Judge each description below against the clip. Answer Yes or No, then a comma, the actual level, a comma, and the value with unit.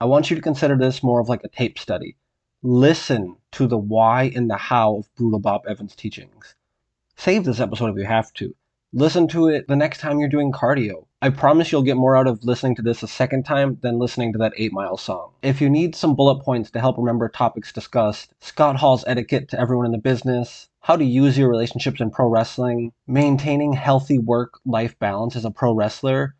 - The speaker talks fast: Yes, fast, 220 wpm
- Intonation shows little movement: No, average, 3.1 semitones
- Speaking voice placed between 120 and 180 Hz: Yes, low, 125 Hz